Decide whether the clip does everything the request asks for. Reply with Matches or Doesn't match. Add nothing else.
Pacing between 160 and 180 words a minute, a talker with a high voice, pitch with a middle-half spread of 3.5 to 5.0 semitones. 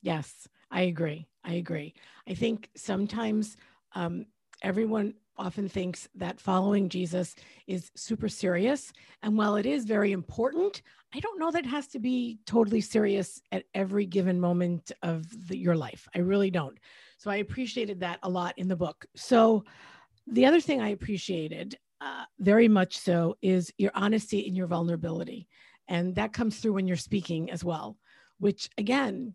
Matches